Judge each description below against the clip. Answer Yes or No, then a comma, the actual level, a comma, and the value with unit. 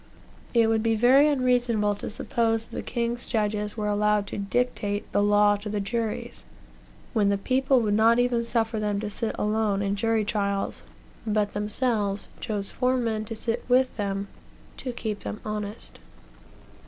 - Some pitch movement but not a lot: No, narrow, 2.3 semitones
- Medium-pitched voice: No, high, 215 Hz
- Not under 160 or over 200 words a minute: Yes, average, 165 wpm